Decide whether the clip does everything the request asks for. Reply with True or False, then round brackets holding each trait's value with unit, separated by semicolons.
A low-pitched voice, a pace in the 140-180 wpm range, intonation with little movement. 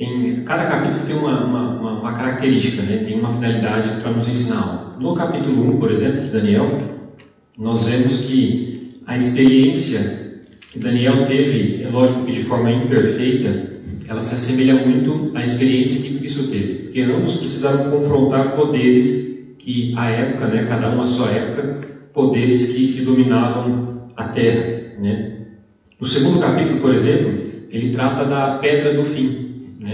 True (125 Hz; 150 wpm; 1.9 semitones)